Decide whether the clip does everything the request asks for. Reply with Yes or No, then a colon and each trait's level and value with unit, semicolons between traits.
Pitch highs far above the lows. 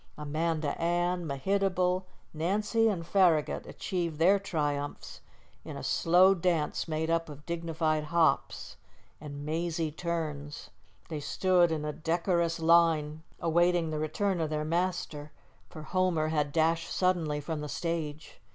No: narrow, 2.4 semitones